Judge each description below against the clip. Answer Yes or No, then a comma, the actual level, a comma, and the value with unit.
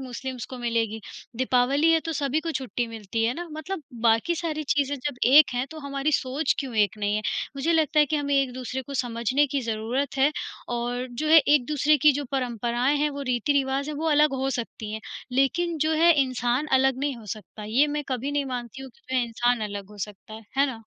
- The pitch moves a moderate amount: Yes, average, 3.6 semitones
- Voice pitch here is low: No, very high, 265 Hz